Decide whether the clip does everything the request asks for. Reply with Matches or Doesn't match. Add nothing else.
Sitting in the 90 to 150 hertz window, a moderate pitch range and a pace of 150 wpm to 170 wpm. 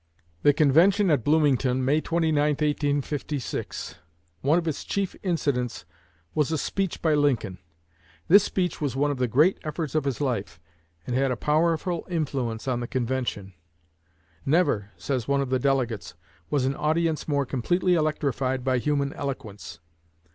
Matches